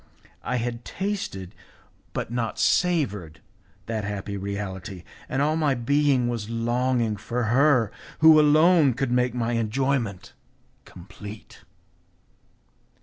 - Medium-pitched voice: No, low, 120 Hz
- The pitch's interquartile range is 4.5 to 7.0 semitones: Yes, average, 5.0 semitones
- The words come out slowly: Yes, slow, 110 wpm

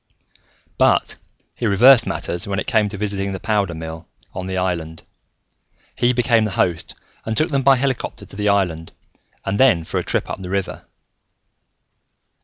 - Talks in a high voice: No, low, 100 Hz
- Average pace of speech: Yes, average, 170 wpm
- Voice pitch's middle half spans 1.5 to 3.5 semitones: No, average, 4.3 semitones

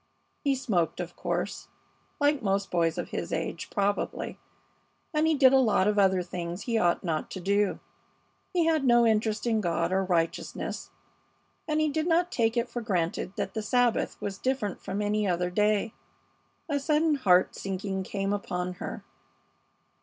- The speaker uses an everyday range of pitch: No, wide, 5.8 semitones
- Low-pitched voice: No, high, 210 Hz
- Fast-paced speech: No, average, 170 wpm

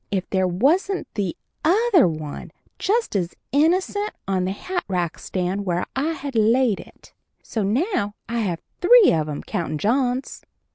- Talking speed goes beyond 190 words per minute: No, average, 150 wpm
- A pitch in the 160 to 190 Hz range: No, high, 220 Hz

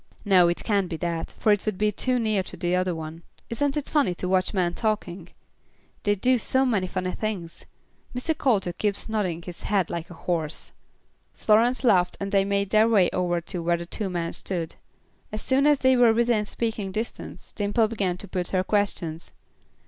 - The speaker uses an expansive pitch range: No, average, 3.8 semitones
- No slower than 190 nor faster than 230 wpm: Yes, average, 195 wpm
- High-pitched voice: Yes, high, 195 Hz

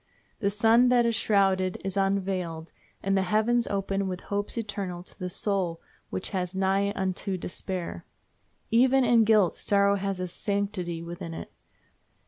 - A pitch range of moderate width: No, narrow, 2.3 semitones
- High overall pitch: Yes, high, 195 Hz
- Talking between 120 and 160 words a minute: Yes, average, 150 wpm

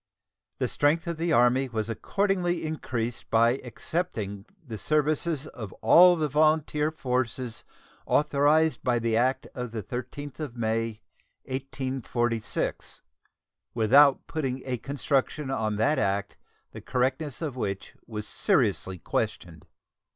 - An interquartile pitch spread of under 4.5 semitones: No, average, 4.8 semitones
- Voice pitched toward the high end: No, low, 130 Hz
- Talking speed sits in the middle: No, slow, 120 wpm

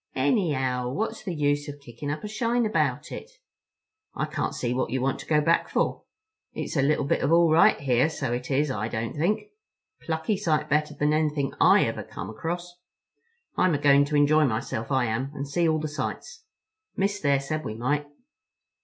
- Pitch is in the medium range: Yes, medium, 145 Hz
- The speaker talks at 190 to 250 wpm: Yes, average, 195 wpm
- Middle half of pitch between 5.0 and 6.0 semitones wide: No, average, 3.5 semitones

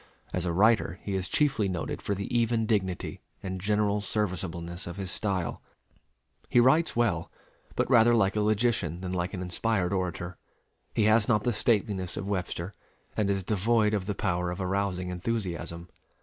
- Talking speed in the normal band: Yes, average, 170 wpm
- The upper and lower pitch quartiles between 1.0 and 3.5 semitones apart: Yes, average, 3.1 semitones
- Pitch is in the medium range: No, low, 100 Hz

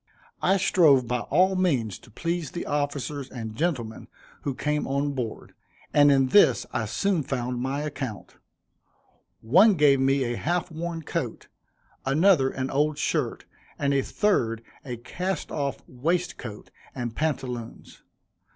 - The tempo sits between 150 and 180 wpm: No, average, 140 wpm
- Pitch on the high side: No, medium, 140 Hz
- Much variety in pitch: No, average, 4.8 semitones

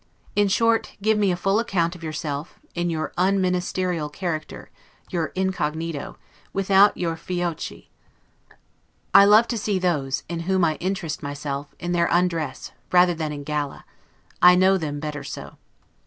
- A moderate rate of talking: Yes, average, 155 wpm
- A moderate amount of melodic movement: Yes, average, 3.6 semitones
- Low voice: No, medium, 175 Hz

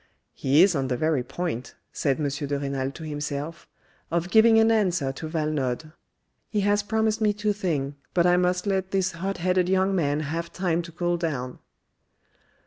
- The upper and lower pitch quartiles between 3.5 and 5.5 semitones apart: Yes, average, 4.7 semitones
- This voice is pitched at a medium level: Yes, medium, 170 Hz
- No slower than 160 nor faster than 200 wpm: Yes, average, 175 wpm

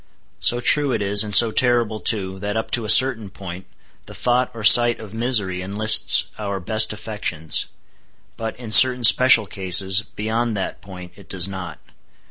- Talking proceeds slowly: No, average, 170 wpm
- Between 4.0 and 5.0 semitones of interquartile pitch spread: No, average, 3.6 semitones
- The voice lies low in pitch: Yes, low, 110 Hz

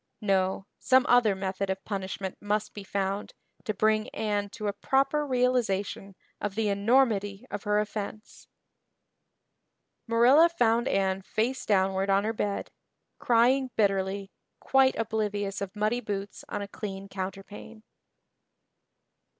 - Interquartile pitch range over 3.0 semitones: No, average, 2.7 semitones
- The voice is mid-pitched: No, high, 205 Hz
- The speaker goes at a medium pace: No, slow, 125 wpm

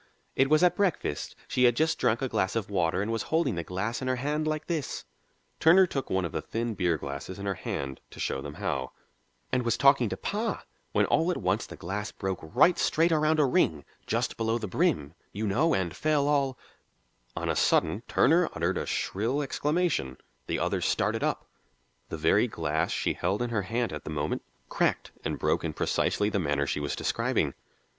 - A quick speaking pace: Yes, fast, 210 wpm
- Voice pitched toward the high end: No, low, 110 Hz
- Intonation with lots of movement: Yes, wide, 8.9 semitones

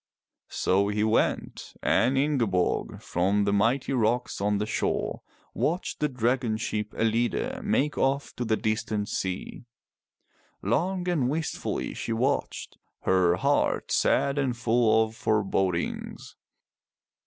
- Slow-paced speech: Yes, slow, 120 wpm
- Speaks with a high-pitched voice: No, low, 115 Hz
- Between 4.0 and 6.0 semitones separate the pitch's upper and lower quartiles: Yes, average, 4.5 semitones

